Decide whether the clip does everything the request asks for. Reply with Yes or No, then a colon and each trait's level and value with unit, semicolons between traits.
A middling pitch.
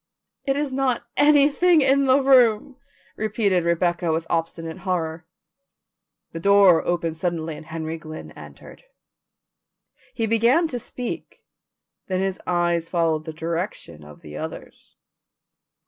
Yes: medium, 180 Hz